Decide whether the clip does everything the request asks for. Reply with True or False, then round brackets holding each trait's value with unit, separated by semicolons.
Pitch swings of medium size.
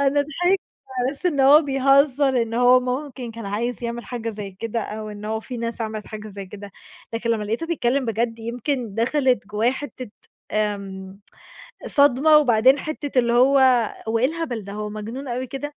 True (4.0 semitones)